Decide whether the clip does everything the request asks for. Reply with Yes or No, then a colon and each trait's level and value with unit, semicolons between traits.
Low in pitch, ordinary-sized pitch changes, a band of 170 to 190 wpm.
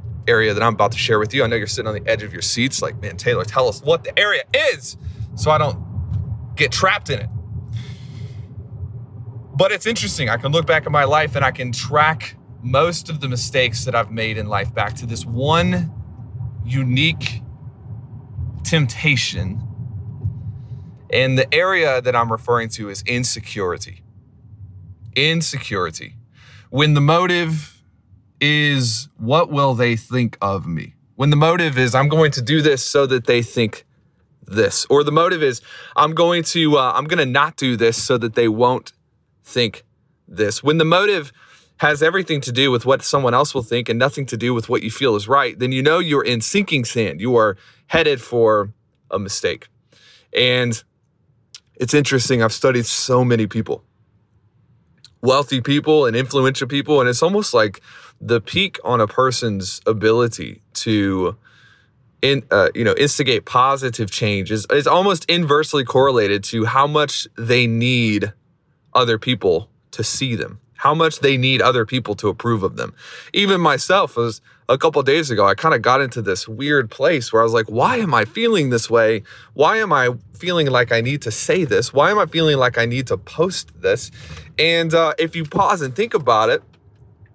Yes: low, 125 Hz; average, 4.6 semitones; average, 180 wpm